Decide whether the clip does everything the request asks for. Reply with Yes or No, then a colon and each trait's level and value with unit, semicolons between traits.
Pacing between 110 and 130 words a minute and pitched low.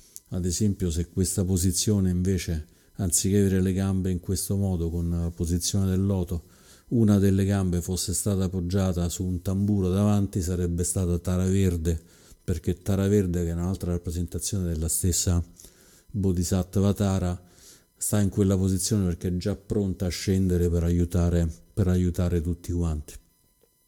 No: average, 150 wpm; very low, 90 Hz